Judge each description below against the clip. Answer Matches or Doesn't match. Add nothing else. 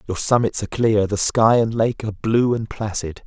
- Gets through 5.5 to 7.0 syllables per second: Doesn't match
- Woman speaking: Doesn't match